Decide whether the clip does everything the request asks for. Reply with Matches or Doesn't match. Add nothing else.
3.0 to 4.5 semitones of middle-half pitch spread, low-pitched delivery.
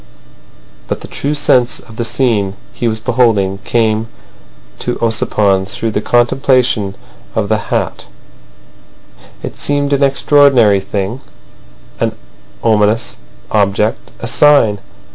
Matches